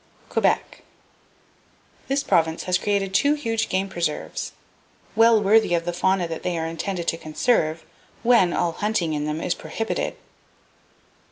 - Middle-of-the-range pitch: Yes, medium, 180 Hz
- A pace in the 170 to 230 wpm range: No, average, 145 wpm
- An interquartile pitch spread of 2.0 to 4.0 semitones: No, average, 4.9 semitones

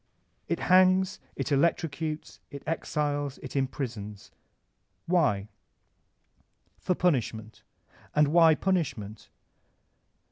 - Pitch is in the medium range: Yes, medium, 150 Hz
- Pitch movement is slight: No, wide, 5.4 semitones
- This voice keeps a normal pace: No, slow, 95 wpm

